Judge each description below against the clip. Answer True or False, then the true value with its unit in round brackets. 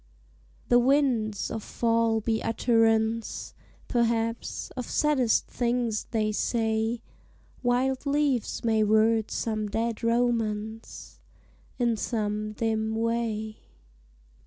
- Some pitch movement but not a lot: False (1.5 semitones)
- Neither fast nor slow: False (95 wpm)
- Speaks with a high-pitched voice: True (225 Hz)